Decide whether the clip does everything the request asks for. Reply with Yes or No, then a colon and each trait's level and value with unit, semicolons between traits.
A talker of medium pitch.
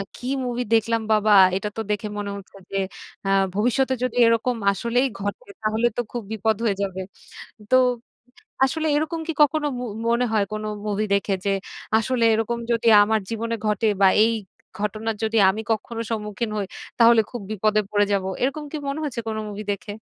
No: high, 225 Hz